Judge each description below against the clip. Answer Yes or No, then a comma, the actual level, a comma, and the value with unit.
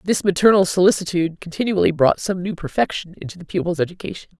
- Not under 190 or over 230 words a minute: No, average, 165 wpm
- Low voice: No, medium, 180 Hz